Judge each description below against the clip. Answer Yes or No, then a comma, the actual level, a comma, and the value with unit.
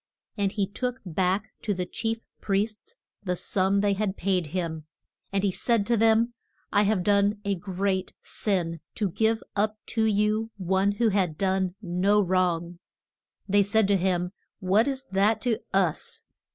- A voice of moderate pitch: No, high, 200 Hz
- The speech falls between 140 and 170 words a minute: Yes, average, 165 wpm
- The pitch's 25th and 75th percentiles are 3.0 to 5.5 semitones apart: No, narrow, 2.5 semitones